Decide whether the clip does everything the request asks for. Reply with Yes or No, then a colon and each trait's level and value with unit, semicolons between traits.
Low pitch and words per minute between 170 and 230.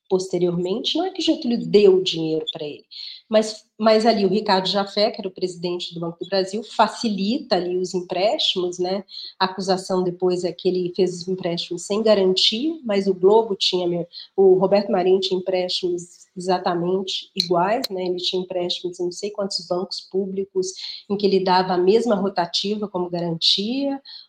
No: high, 190 Hz; average, 175 wpm